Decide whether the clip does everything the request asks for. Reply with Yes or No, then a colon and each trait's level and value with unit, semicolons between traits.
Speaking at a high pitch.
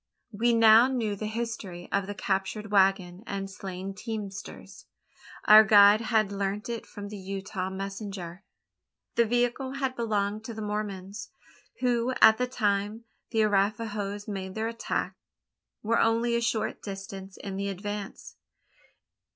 Yes: high, 205 Hz